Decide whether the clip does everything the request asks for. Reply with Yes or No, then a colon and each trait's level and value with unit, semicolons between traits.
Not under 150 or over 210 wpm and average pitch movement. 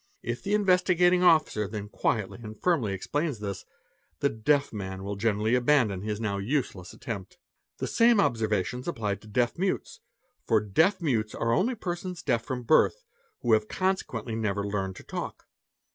No: average, 165 wpm; wide, 7.4 semitones